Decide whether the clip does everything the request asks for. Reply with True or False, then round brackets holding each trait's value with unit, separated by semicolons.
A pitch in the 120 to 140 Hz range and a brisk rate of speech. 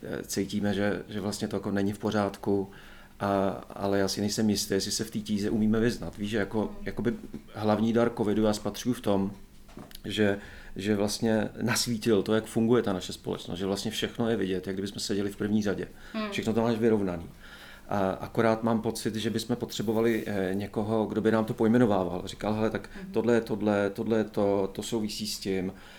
False (105 Hz; 195 wpm)